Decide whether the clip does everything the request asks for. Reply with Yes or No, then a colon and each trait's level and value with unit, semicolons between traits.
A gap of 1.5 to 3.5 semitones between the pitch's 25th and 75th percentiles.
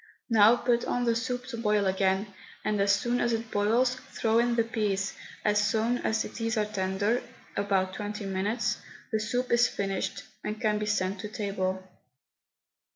Yes: average, 2.8 semitones